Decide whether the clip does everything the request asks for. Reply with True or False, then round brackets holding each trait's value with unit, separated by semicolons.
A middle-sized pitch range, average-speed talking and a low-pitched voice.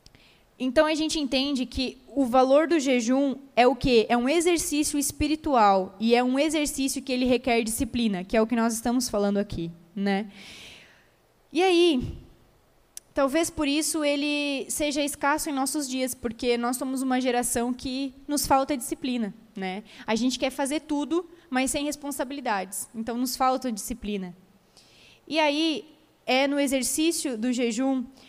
False (3.5 semitones; 155 wpm; 265 Hz)